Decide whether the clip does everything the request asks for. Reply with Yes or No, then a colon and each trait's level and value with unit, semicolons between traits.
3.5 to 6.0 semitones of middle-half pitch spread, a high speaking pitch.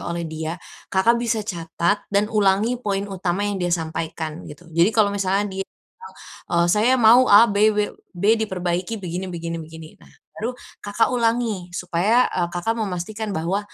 Yes: average, 3.9 semitones; high, 195 Hz